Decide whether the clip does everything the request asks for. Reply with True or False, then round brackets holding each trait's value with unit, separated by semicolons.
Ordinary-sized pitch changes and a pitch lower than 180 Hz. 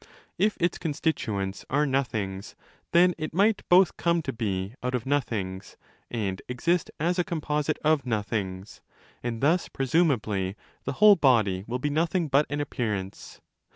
False (7.5 semitones; 135 Hz)